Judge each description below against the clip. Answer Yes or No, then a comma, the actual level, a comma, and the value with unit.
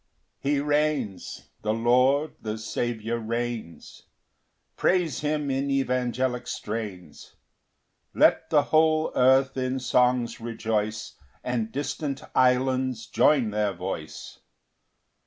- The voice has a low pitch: Yes, low, 125 Hz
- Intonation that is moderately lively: Yes, average, 3.5 semitones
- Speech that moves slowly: Yes, slow, 100 wpm